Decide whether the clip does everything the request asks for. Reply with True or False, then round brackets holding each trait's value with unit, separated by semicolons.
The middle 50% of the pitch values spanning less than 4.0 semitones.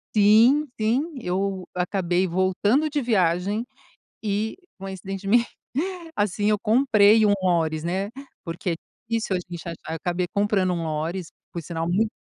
True (3.4 semitones)